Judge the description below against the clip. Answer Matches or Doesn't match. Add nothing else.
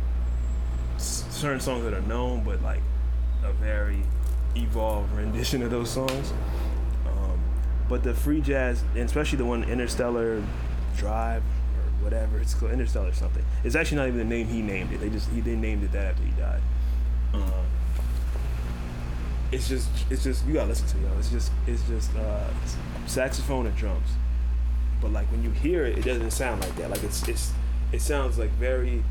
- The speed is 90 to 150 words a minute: Doesn't match